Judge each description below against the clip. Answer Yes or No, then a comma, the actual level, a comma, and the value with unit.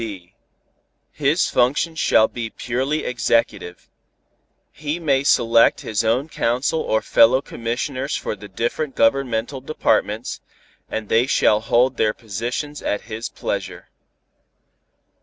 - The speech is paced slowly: Yes, slow, 120 wpm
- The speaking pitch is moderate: No, low, 120 Hz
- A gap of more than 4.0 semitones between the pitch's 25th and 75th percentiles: No, average, 3.6 semitones